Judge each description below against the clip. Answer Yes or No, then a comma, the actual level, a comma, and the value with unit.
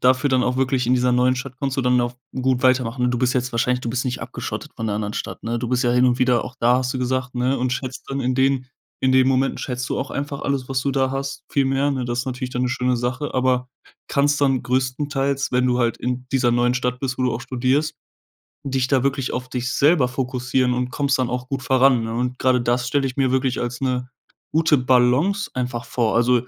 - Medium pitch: No, low, 125 Hz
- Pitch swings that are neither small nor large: No, narrow, 1.2 semitones